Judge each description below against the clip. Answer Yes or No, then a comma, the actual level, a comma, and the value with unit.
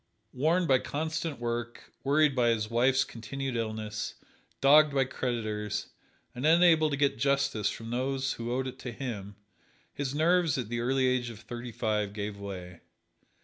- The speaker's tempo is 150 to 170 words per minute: Yes, average, 160 wpm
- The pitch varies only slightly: No, average, 3.7 semitones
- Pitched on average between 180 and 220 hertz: No, low, 125 Hz